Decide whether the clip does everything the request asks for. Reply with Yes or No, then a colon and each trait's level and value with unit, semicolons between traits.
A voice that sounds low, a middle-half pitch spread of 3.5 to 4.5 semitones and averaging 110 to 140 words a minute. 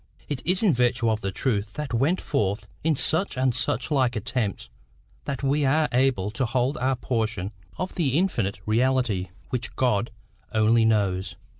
No: low, 125 Hz; average, 4.0 semitones; average, 165 wpm